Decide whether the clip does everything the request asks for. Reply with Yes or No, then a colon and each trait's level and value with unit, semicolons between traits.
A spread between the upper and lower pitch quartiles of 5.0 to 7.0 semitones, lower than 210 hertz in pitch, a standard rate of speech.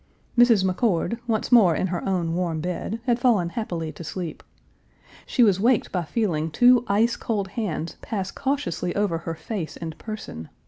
Yes: average, 5.3 semitones; high, 190 Hz; average, 170 wpm